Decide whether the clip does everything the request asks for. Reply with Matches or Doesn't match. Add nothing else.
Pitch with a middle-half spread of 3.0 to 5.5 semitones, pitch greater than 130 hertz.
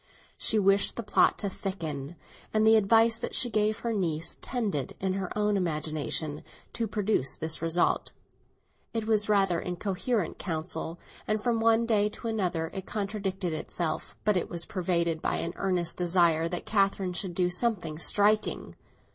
Matches